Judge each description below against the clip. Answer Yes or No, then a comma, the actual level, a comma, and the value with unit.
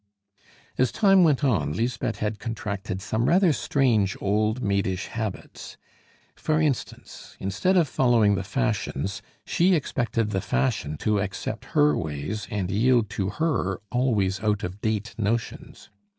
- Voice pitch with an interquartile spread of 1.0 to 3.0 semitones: No, average, 4.6 semitones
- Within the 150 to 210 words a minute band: No, slow, 135 wpm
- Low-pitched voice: Yes, low, 110 Hz